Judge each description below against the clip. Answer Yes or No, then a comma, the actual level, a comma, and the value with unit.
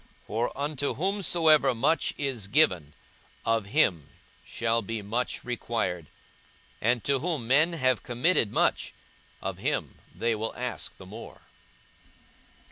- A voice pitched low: Yes, low, 120 Hz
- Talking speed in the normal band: No, slow, 125 wpm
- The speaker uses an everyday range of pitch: Yes, average, 4.6 semitones